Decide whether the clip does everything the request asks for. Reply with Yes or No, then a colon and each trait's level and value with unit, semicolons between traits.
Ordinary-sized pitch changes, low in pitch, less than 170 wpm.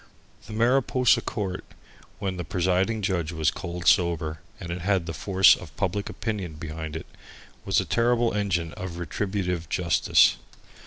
Yes: average, 3.6 semitones; very low, 90 Hz; average, 150 wpm